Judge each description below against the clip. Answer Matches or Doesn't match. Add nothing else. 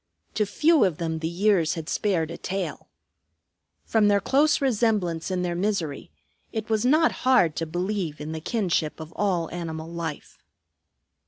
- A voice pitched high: Doesn't match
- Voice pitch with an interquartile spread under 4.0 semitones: Doesn't match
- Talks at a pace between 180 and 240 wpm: Doesn't match